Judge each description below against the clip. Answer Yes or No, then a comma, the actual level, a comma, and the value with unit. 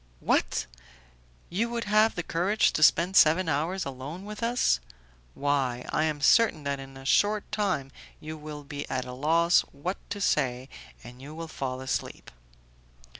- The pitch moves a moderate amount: No, wide, 5.7 semitones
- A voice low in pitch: No, medium, 155 Hz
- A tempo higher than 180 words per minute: No, average, 165 wpm